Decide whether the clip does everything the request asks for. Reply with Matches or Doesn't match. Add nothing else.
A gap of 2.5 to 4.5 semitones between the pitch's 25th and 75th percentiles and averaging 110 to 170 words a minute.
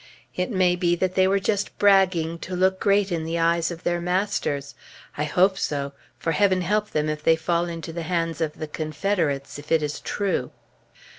Doesn't match